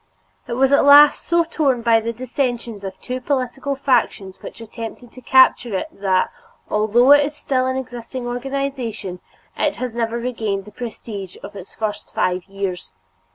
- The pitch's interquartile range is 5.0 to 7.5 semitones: No, average, 3.8 semitones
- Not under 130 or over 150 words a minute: No, average, 165 wpm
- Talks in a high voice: Yes, high, 240 Hz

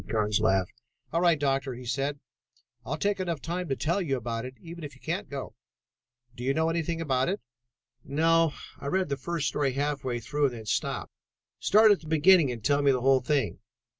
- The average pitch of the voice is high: No, medium, 145 Hz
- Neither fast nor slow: No, fast, 210 wpm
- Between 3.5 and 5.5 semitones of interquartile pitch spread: Yes, average, 4.3 semitones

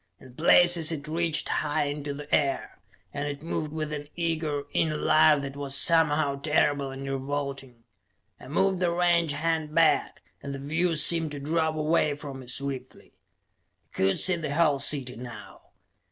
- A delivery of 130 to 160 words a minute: No, average, 170 wpm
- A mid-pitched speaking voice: Yes, medium, 150 Hz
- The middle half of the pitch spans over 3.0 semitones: No, narrow, 2.6 semitones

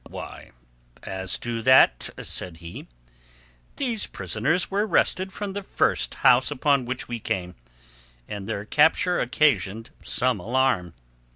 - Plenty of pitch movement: Yes, wide, 7.8 semitones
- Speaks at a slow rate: Yes, slow, 125 wpm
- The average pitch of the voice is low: Yes, low, 125 Hz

